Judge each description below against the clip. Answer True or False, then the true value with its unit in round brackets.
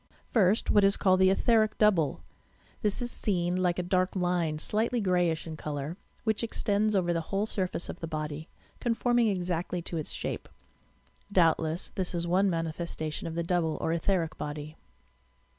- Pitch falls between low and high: True (180 Hz)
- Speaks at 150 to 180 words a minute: True (170 wpm)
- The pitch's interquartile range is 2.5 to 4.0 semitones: True (3.5 semitones)